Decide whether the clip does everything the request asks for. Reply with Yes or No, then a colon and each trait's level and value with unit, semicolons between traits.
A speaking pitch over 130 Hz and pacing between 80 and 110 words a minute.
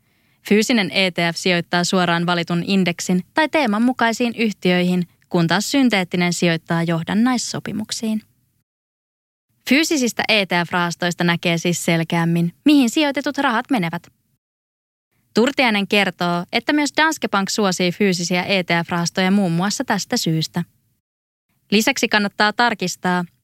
Yes: medium, 185 Hz; average, 100 wpm